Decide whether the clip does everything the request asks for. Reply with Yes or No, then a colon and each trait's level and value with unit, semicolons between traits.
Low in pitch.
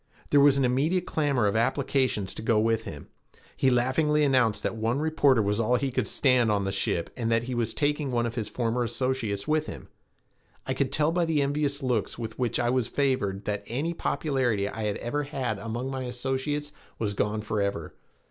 Yes: low, 125 Hz